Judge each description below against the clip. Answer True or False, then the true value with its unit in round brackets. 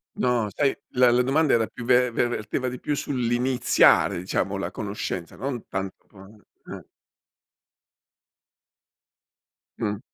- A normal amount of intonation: True (3.2 semitones)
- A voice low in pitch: True (120 Hz)